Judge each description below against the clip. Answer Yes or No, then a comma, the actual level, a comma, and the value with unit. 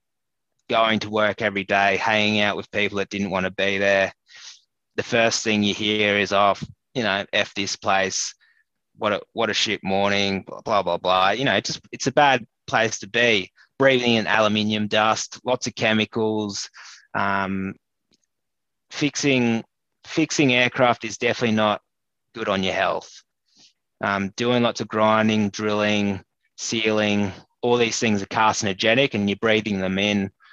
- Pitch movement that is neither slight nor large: No, narrow, 2.3 semitones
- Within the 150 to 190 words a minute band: Yes, average, 160 wpm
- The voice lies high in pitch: No, low, 105 Hz